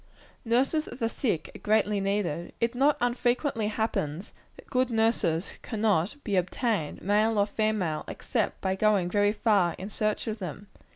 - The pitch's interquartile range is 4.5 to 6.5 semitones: No, average, 3.2 semitones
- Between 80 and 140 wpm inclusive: No, average, 160 wpm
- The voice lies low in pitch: No, high, 210 Hz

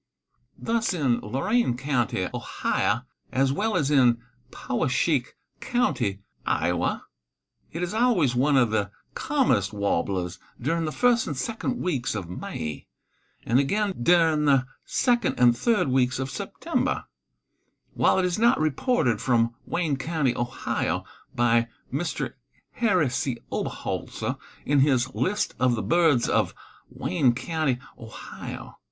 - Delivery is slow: Yes, slow, 130 wpm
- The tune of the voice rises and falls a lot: Yes, wide, 6.5 semitones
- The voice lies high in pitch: No, low, 135 Hz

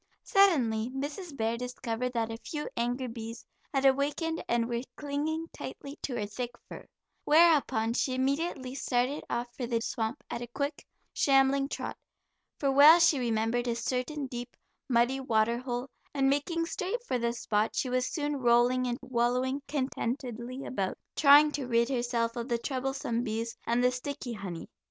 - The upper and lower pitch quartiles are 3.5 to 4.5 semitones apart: No, average, 3.0 semitones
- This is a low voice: No, very high, 250 Hz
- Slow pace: No, average, 165 wpm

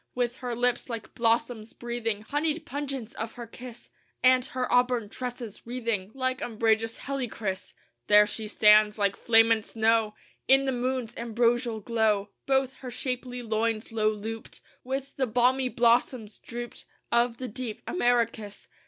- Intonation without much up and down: Yes, narrow, 2.3 semitones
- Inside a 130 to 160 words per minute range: Yes, average, 145 wpm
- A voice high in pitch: Yes, high, 235 Hz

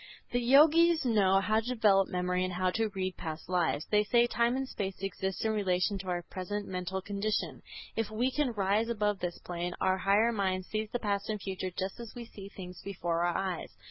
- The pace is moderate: No, fast, 210 wpm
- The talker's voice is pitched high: Yes, high, 200 Hz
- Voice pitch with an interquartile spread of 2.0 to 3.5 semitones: Yes, average, 3.2 semitones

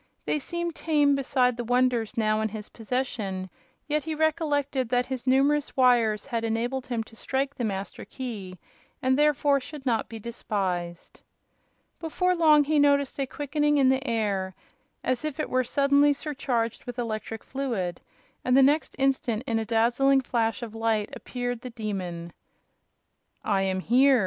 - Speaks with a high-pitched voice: Yes, very high, 250 Hz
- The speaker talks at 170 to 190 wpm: No, average, 160 wpm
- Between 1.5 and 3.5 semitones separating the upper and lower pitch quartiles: No, average, 4.0 semitones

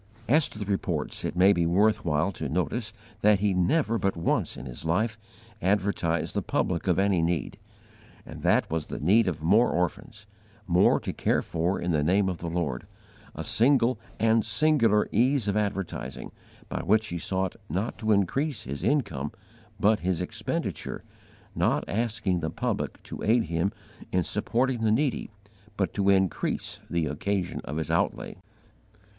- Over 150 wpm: Yes, average, 165 wpm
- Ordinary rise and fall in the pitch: Yes, average, 4.4 semitones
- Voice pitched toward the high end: No, very low, 95 Hz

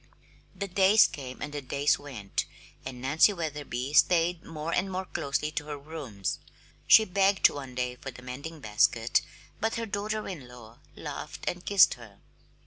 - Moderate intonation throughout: No, wide, 6.4 semitones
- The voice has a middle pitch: Yes, medium, 150 Hz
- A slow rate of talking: No, average, 165 wpm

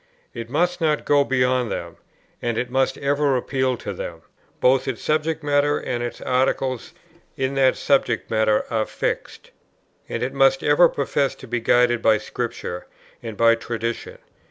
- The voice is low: Yes, low, 130 Hz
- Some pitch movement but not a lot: Yes, average, 3.2 semitones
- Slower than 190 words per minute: Yes, average, 160 wpm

